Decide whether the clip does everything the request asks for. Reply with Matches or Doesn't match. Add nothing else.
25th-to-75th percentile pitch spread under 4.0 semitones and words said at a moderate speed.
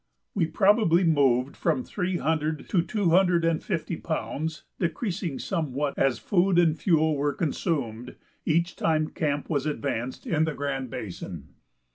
Matches